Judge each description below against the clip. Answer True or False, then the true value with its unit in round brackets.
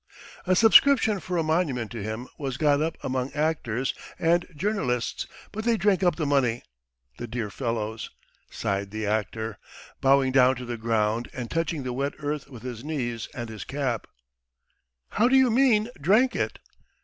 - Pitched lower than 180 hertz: True (135 Hz)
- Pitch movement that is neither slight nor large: False (6.4 semitones)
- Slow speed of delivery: False (175 wpm)